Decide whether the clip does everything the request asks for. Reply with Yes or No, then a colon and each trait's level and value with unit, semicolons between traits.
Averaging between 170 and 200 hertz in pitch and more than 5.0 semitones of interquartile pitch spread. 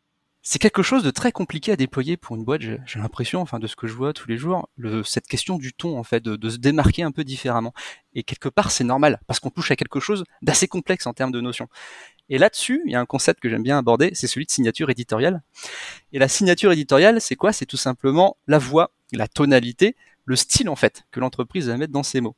No: low, 135 Hz; wide, 5.5 semitones